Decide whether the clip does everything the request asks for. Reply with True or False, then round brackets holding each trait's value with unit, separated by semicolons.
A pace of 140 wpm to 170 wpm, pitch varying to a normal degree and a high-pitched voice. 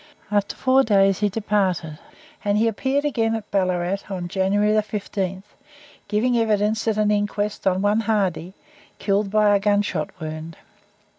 False (145 wpm; 2.0 semitones; 205 Hz)